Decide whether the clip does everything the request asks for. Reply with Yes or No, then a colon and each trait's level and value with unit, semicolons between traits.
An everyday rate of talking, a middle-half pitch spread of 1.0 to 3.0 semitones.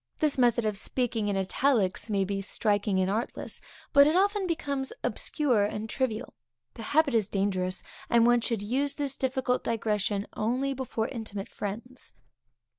No: average, 155 wpm; average, 4.5 semitones